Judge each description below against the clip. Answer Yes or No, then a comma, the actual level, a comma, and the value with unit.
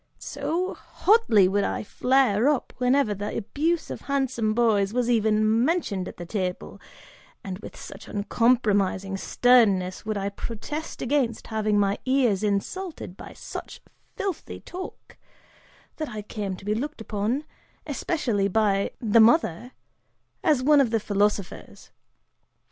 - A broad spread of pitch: No, average, 4.7 semitones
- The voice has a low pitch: No, high, 220 Hz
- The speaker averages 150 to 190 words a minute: No, slow, 135 wpm